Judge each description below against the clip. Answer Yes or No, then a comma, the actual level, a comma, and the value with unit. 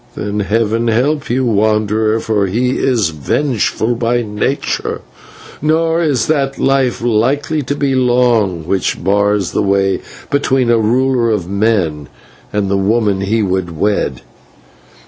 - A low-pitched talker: Yes, low, 110 Hz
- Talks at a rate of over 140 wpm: No, slow, 135 wpm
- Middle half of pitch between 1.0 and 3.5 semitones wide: No, average, 4.4 semitones